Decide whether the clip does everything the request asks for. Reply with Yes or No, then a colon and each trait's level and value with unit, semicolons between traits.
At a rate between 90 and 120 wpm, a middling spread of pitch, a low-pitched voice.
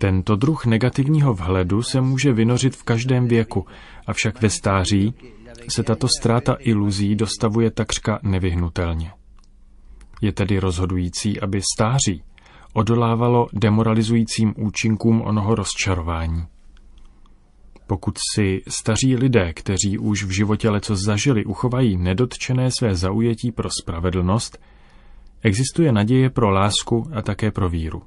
Yes: slow, 115 wpm; average, 3.5 semitones; low, 105 Hz